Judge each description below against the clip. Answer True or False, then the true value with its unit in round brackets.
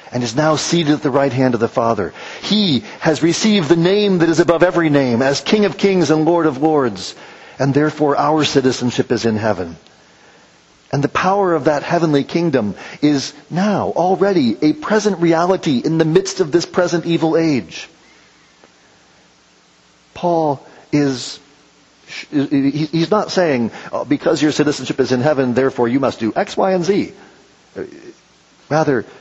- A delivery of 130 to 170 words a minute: True (160 wpm)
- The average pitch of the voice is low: False (150 Hz)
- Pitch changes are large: False (4.6 semitones)